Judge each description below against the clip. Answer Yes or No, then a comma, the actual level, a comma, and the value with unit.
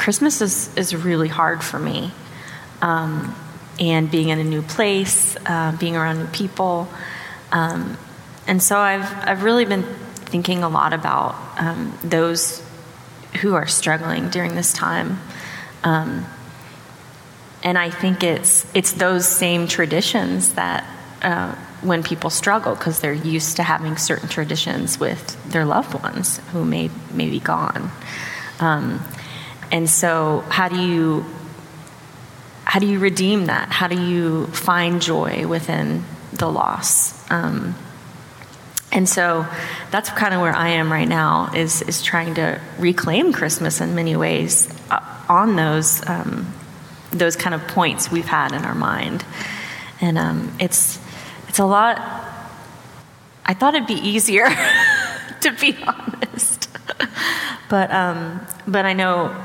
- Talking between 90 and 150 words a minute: Yes, average, 140 wpm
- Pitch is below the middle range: No, medium, 170 Hz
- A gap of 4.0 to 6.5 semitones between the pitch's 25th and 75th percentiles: No, average, 2.9 semitones